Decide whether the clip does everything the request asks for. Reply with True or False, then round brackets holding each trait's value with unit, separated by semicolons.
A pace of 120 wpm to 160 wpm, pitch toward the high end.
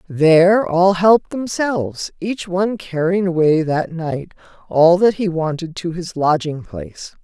False (150 wpm; 175 Hz)